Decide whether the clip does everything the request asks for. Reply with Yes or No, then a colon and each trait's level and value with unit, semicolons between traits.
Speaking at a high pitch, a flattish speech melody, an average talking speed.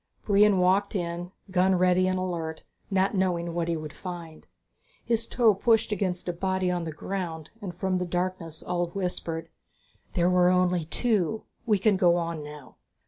No: medium, 180 Hz; narrow, 2.0 semitones; average, 170 wpm